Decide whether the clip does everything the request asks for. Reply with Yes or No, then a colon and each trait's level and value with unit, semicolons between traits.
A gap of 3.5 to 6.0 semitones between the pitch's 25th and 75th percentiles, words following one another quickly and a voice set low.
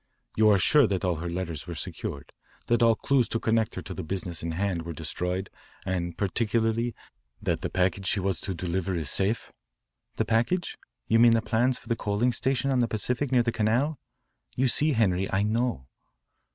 No: average, 4.4 semitones; average, 195 wpm; low, 110 Hz